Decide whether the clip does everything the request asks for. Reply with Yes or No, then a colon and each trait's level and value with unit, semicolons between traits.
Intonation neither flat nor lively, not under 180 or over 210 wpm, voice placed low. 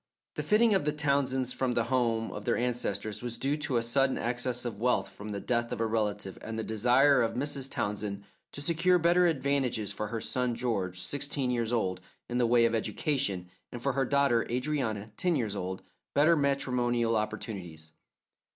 Yes: average, 4.1 semitones; average, 190 wpm; low, 120 Hz